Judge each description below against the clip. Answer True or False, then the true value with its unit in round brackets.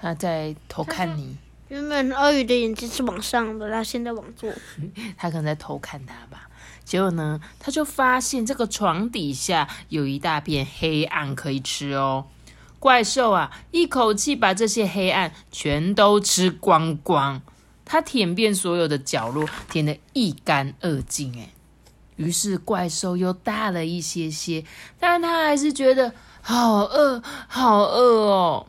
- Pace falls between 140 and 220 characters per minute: True (215 characters per minute)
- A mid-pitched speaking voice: False (195 Hz)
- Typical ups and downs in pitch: False (7.2 semitones)